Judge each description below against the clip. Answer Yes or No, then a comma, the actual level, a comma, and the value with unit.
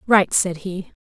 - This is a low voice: No, medium, 185 Hz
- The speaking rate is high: No, average, 175 wpm